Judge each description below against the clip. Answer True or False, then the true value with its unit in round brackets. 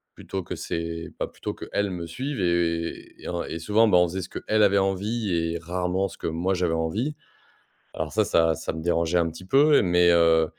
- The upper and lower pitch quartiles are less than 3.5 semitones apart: True (2.9 semitones)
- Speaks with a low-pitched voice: True (90 Hz)